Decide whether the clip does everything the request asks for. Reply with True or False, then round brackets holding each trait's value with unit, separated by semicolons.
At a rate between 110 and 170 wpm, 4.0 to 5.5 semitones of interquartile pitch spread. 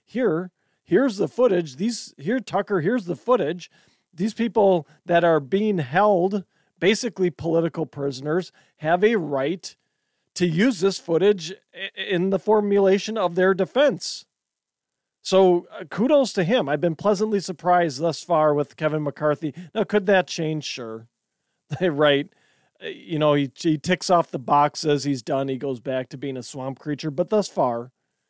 True (160 wpm; 4.8 semitones)